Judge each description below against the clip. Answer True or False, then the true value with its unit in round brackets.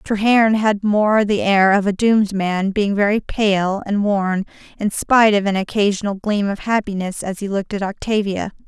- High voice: True (205 Hz)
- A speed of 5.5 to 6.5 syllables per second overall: False (4.9 syllables/s)